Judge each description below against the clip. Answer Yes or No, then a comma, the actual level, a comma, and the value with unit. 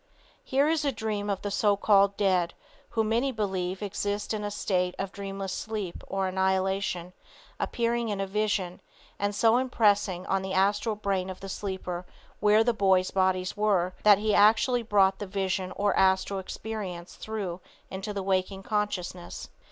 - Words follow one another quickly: No, average, 165 wpm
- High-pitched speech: Yes, high, 200 Hz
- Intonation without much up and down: Yes, narrow, 2.0 semitones